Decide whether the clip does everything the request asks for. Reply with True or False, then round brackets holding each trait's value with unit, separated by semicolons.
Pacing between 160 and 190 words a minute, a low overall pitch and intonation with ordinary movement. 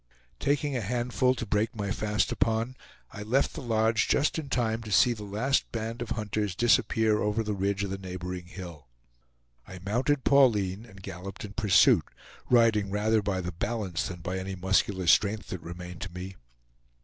True (180 wpm; 105 Hz; 3.5 semitones)